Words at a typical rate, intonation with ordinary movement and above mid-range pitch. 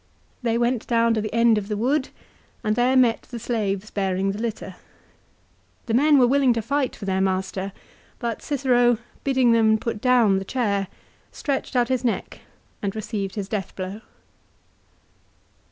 Yes: average, 165 wpm; average, 3.6 semitones; high, 230 Hz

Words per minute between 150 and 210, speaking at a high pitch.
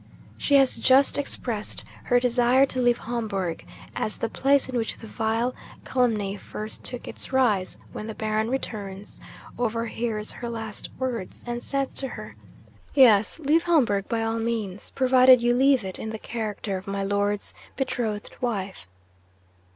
Yes: average, 155 wpm; high, 230 Hz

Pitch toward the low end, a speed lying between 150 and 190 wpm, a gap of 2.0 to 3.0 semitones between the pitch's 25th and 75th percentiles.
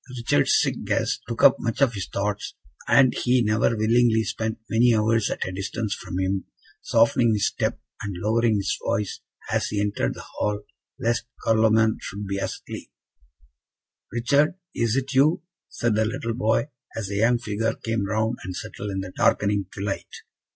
Yes: low, 110 Hz; average, 170 wpm; narrow, 2.4 semitones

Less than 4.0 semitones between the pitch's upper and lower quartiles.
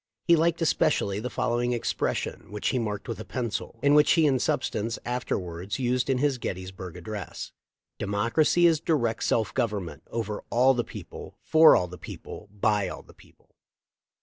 No: average, 4.7 semitones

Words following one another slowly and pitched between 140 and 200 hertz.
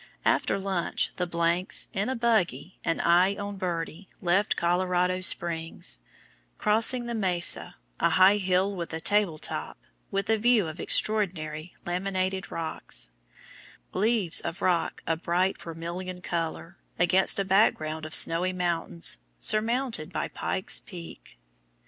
Yes: slow, 130 wpm; medium, 185 Hz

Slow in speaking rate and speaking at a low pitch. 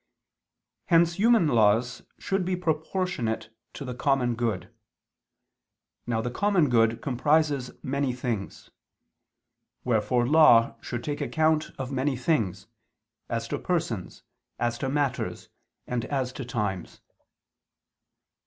Yes: slow, 115 wpm; low, 125 Hz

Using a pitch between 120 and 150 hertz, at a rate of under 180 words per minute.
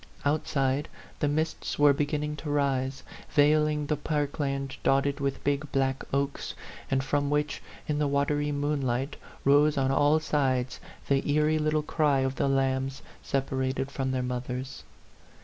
Yes: medium, 140 Hz; average, 150 wpm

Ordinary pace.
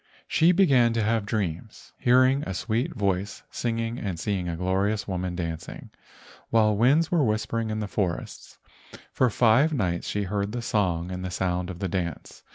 Yes: average, 170 wpm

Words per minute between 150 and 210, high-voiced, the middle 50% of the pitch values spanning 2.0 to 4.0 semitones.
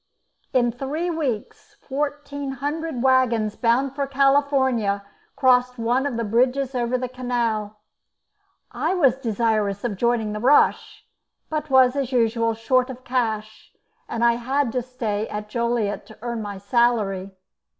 No: average, 140 wpm; high, 245 Hz; average, 3.2 semitones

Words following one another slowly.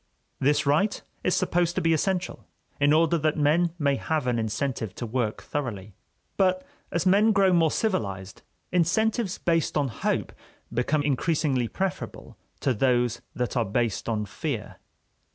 No: average, 150 wpm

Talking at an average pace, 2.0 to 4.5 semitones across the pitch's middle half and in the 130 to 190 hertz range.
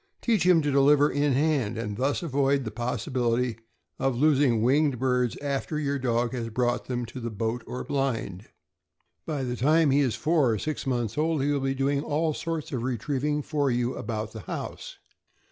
Yes: average, 190 wpm; average, 3.4 semitones; low, 135 Hz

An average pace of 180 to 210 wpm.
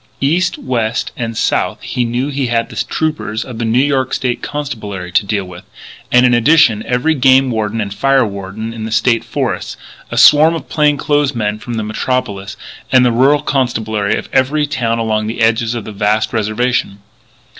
Yes: average, 190 wpm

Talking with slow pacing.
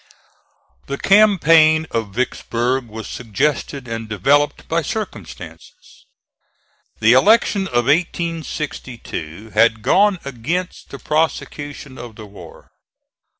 Yes: slow, 100 wpm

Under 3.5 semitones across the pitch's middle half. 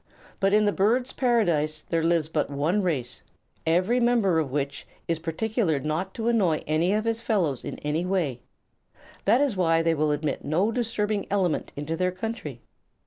No: wide, 5.6 semitones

